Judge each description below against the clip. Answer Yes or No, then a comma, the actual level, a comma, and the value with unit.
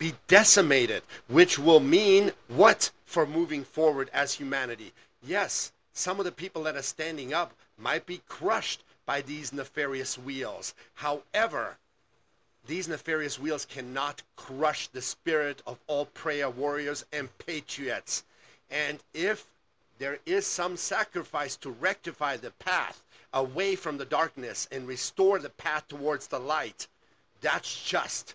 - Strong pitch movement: No, average, 4.6 semitones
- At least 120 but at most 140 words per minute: Yes, slow, 135 wpm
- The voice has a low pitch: No, medium, 150 Hz